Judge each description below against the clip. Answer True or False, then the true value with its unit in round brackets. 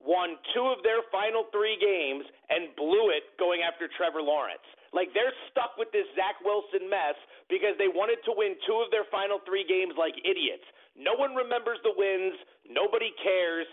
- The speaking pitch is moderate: False (205 Hz)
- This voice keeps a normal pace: True (185 wpm)